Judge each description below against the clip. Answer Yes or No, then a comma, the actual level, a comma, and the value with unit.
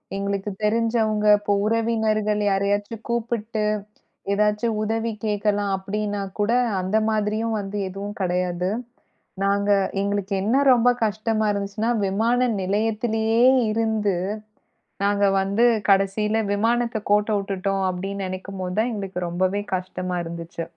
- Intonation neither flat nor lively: No, narrow, 2.0 semitones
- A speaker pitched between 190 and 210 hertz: Yes, high, 205 Hz